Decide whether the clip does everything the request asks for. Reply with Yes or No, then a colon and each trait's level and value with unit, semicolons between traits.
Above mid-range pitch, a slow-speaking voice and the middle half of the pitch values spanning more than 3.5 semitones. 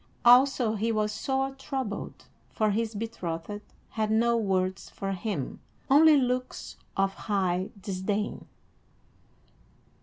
Yes: high, 215 Hz; slow, 110 wpm; average, 3.9 semitones